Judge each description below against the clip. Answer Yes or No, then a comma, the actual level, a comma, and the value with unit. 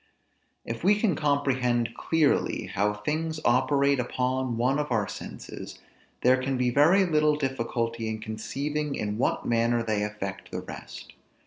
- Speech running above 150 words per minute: No, average, 145 wpm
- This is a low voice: Yes, low, 130 Hz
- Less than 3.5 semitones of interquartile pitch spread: No, average, 4.3 semitones